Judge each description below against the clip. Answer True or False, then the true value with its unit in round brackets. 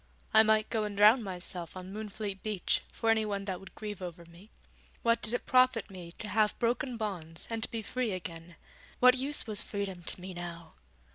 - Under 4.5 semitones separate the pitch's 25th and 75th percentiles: True (3.6 semitones)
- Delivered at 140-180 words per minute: False (200 wpm)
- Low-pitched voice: False (210 Hz)